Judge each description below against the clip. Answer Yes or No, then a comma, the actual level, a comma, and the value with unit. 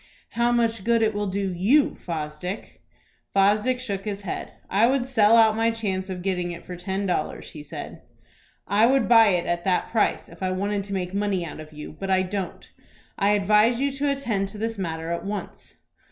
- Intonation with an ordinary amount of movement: Yes, average, 3.6 semitones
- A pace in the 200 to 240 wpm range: Yes, fast, 205 wpm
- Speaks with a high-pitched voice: Yes, high, 200 Hz